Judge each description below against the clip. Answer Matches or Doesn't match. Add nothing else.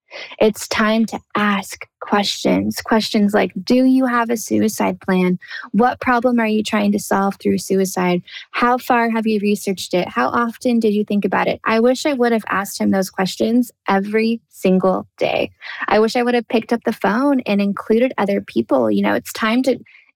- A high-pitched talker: Matches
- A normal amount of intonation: Matches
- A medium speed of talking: Matches